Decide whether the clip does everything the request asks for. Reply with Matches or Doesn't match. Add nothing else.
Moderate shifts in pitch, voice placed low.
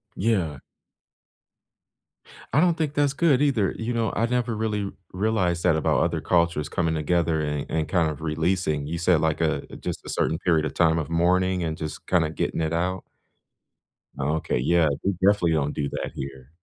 Matches